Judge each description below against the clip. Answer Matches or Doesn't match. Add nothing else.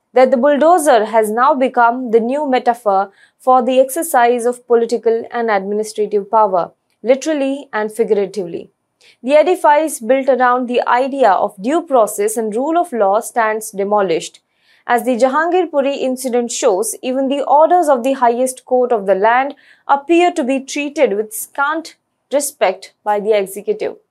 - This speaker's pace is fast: Doesn't match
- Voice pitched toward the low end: Doesn't match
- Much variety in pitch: Doesn't match